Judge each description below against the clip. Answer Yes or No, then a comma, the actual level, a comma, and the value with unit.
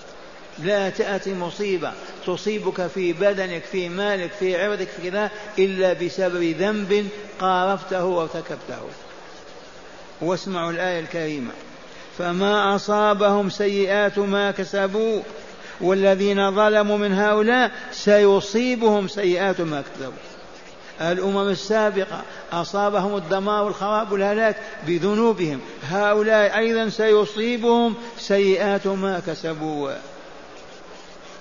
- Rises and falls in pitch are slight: Yes, narrow, 2.2 semitones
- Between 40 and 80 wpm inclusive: No, average, 90 wpm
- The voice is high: Yes, high, 200 Hz